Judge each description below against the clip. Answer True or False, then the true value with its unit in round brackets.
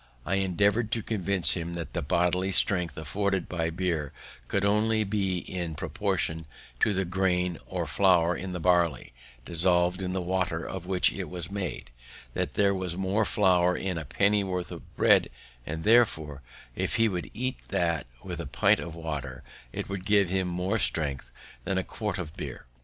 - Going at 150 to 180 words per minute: True (175 wpm)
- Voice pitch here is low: True (90 Hz)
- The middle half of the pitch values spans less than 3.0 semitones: True (2.6 semitones)